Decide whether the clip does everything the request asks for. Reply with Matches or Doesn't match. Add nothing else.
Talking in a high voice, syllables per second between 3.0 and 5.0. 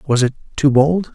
Doesn't match